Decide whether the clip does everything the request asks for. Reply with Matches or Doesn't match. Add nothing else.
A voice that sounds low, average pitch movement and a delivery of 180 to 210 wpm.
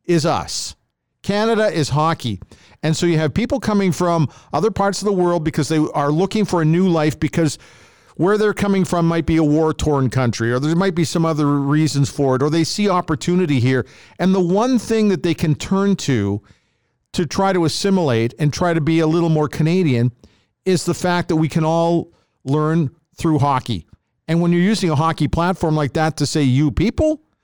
Doesn't match